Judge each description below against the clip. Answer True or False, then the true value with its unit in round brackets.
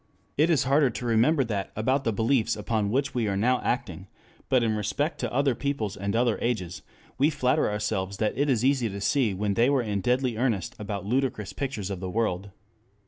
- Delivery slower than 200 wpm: False (205 wpm)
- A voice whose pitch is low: True (115 Hz)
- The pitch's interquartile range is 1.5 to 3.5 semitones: False (4.5 semitones)